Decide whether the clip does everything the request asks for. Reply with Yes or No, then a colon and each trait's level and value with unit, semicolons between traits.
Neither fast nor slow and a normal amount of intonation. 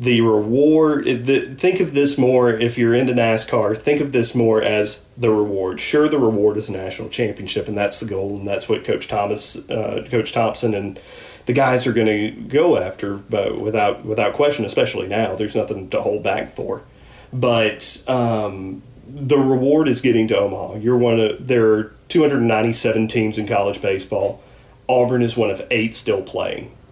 Yes: average, 185 wpm; average, 3.0 semitones